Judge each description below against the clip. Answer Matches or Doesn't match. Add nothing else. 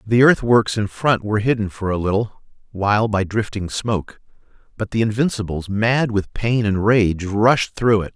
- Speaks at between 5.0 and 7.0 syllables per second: Doesn't match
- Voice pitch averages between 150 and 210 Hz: Doesn't match